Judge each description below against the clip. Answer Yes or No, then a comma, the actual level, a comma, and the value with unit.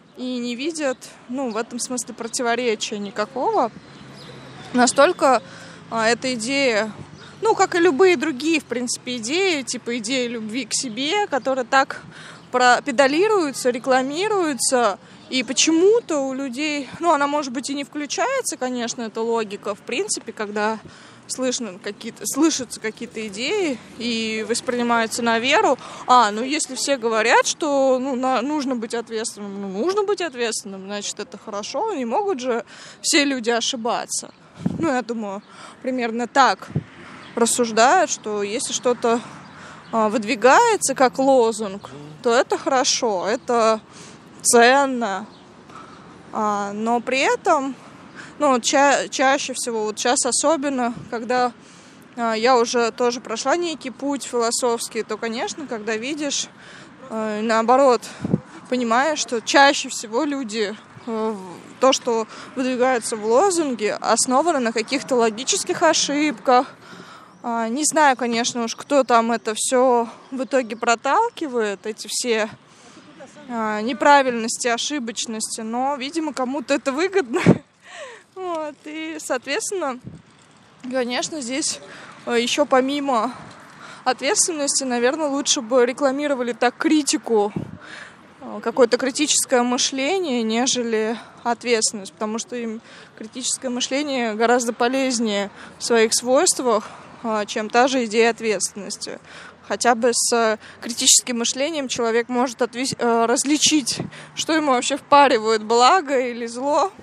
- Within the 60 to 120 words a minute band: Yes, average, 115 wpm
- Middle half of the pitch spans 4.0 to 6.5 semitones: No, average, 3.5 semitones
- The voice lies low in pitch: No, very high, 250 Hz